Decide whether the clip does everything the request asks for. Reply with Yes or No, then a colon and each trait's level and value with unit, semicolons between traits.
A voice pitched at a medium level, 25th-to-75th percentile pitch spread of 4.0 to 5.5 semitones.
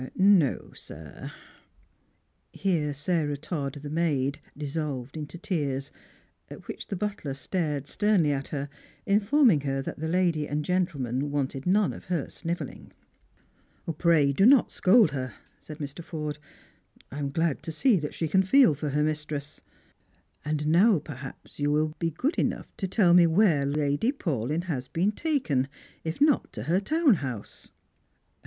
Yes: medium, 155 Hz; average, 4.4 semitones